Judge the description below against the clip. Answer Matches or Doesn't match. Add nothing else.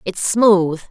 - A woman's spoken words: Matches